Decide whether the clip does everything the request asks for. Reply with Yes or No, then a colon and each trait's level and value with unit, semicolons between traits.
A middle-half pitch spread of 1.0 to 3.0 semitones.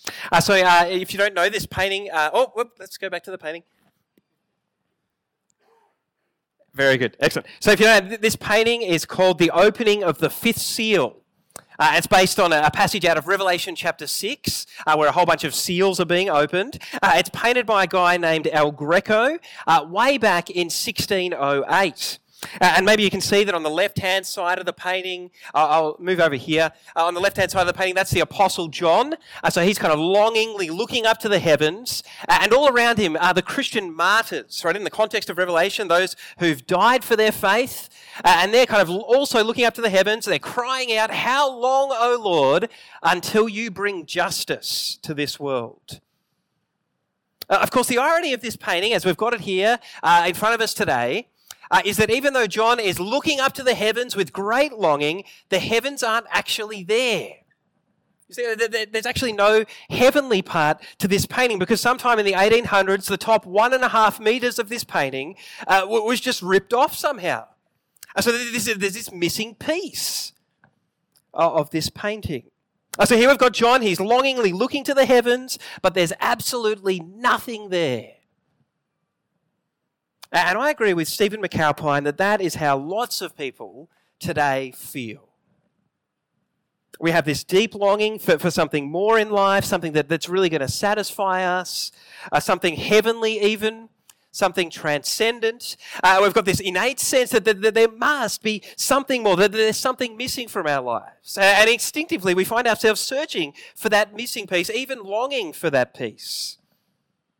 No: average, 4.6 semitones